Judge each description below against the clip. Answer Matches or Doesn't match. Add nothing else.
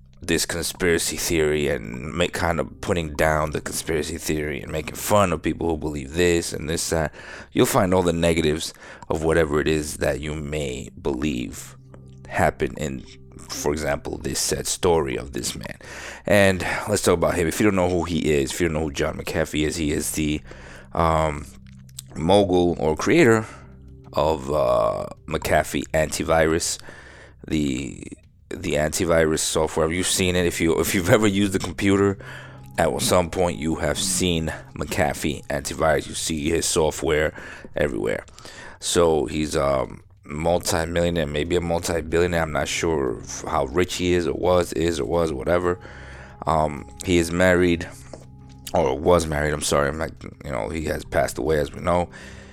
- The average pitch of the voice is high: Doesn't match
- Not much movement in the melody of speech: Doesn't match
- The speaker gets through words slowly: Doesn't match